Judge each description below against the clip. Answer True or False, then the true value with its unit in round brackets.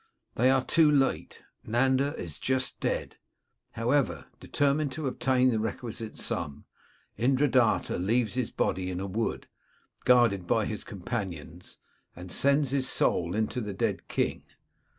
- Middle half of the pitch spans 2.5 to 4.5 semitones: False (5.1 semitones)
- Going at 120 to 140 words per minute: True (135 wpm)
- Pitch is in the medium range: False (120 Hz)